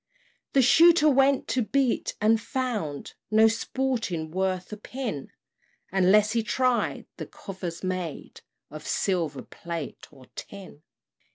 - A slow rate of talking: Yes, slow, 120 wpm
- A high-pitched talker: Yes, high, 210 Hz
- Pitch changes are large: Yes, wide, 6.4 semitones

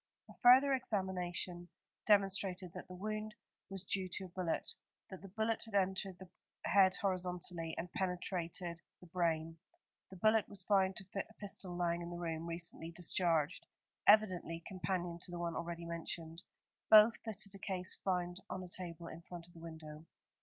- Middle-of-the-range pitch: Yes, medium, 180 Hz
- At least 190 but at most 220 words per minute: No, average, 170 wpm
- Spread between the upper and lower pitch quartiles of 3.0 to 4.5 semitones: No, narrow, 2.4 semitones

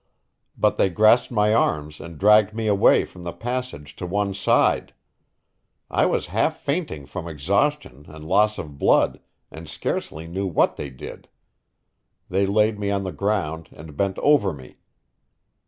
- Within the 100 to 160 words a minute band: Yes, average, 155 wpm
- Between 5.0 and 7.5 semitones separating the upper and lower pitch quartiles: Yes, average, 5.3 semitones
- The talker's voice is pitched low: Yes, very low, 95 Hz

